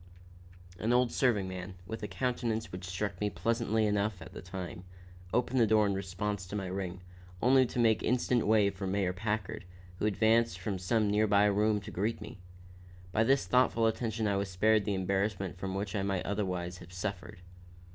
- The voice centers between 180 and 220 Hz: No, low, 105 Hz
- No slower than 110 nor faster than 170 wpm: No, average, 190 wpm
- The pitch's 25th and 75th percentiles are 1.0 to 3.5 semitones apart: Yes, average, 3.0 semitones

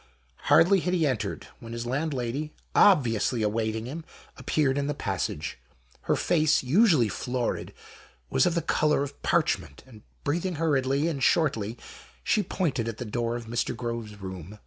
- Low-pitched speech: Yes, low, 130 Hz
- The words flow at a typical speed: Yes, average, 155 wpm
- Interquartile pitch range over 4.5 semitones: Yes, average, 5.3 semitones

